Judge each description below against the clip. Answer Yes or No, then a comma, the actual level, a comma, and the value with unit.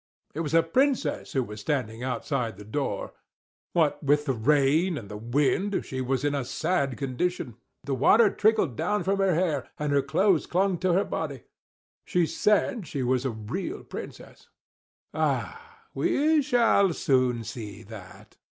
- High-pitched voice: No, medium, 145 Hz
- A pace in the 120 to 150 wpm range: No, average, 160 wpm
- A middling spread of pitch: No, wide, 6.8 semitones